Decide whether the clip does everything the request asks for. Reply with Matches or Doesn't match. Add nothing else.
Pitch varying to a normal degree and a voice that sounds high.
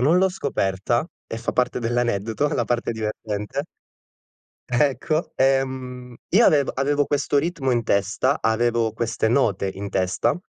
Doesn't match